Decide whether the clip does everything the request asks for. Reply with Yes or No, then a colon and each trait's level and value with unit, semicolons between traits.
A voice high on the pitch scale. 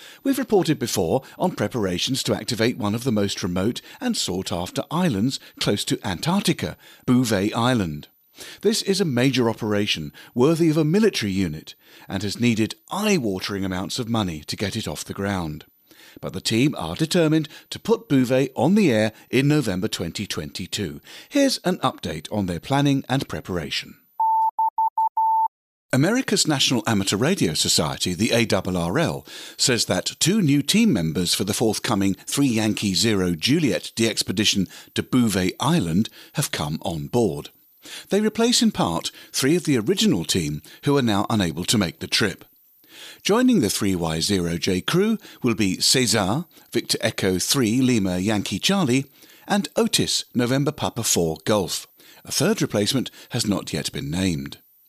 No: low, 115 Hz